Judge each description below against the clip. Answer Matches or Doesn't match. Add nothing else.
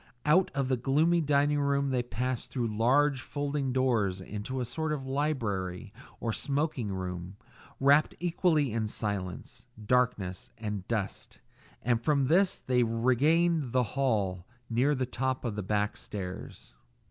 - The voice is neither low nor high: Doesn't match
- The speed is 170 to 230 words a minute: Doesn't match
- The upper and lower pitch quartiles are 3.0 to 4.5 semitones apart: Doesn't match